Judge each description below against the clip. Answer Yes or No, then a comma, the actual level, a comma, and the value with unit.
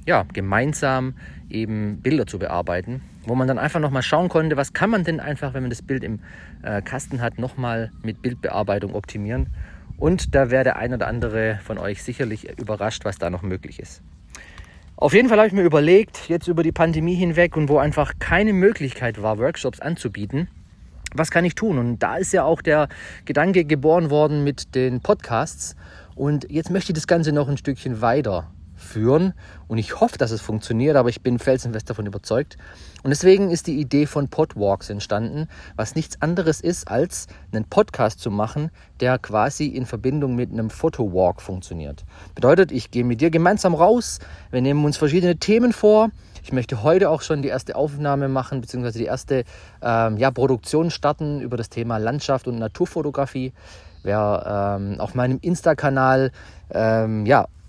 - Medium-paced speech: Yes, average, 180 wpm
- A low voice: Yes, low, 130 Hz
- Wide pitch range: Yes, wide, 6.1 semitones